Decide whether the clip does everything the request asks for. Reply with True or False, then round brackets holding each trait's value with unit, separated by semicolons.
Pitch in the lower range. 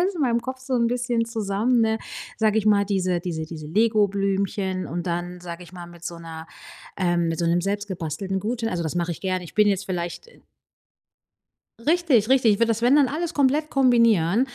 False (200 Hz)